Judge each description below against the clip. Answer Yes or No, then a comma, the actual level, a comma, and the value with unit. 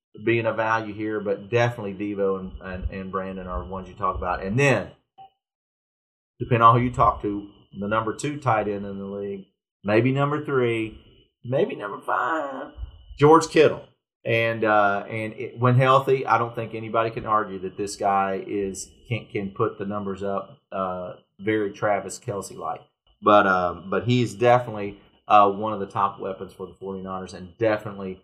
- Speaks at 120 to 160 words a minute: No, average, 175 wpm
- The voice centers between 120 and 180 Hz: No, low, 105 Hz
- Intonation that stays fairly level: No, average, 3.0 semitones